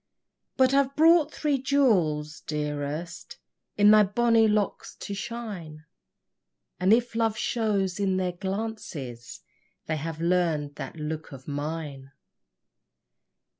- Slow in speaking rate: Yes, slow, 115 wpm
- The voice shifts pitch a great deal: Yes, wide, 6.7 semitones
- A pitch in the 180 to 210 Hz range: Yes, medium, 185 Hz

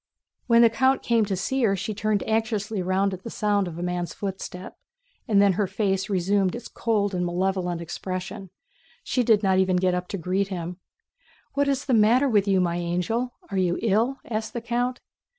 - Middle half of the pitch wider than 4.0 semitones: No, average, 3.4 semitones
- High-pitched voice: Yes, high, 200 Hz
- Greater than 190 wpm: Yes, average, 200 wpm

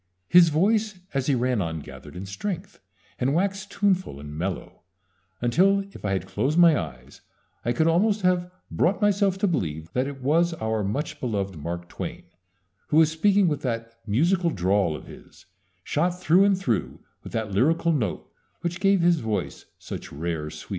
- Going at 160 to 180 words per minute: Yes, average, 175 wpm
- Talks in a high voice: No, medium, 150 Hz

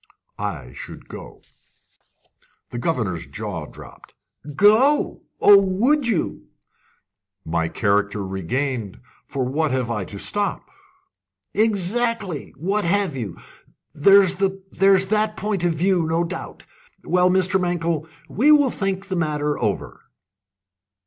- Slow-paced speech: Yes, slow, 110 wpm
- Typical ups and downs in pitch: No, wide, 8.4 semitones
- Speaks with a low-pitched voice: No, medium, 175 Hz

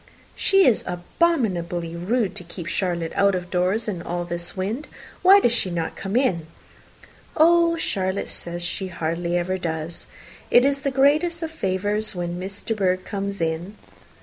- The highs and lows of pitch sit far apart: Yes, wide, 5.7 semitones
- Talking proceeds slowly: No, average, 165 wpm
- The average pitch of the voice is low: No, high, 190 Hz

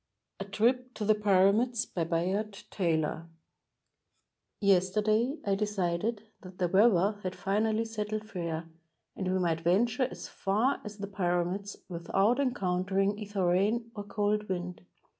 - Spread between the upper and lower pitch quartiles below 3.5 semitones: Yes, average, 2.9 semitones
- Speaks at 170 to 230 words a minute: No, average, 140 wpm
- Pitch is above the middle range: Yes, high, 200 Hz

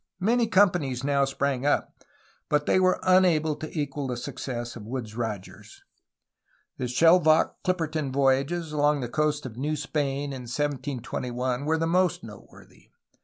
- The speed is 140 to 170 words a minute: Yes, average, 150 wpm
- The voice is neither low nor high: Yes, medium, 145 Hz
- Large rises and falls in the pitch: No, average, 3.7 semitones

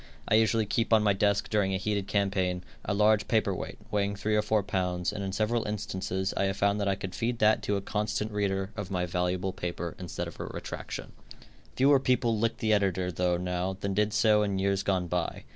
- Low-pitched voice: Yes, low, 100 Hz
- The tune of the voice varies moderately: No, narrow, 2.2 semitones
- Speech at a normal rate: No, fast, 220 wpm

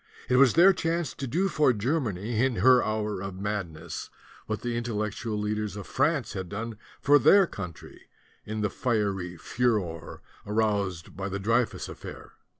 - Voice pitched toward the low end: Yes, low, 110 Hz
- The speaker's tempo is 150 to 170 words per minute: Yes, average, 160 wpm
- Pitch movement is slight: No, average, 4.2 semitones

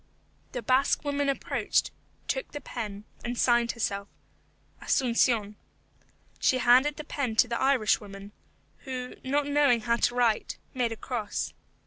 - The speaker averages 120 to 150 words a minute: Yes, average, 140 wpm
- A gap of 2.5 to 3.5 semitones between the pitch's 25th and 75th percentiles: Yes, average, 3.1 semitones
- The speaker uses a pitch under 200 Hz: No, high, 245 Hz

